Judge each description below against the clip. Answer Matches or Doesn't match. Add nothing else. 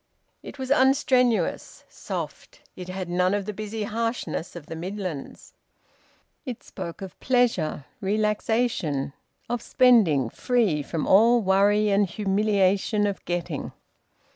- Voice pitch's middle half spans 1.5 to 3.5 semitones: Doesn't match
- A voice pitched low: Doesn't match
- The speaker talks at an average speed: Doesn't match